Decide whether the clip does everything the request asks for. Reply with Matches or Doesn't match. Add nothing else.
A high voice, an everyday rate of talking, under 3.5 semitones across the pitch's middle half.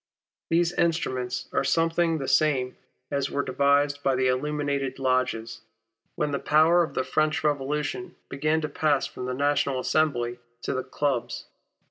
Doesn't match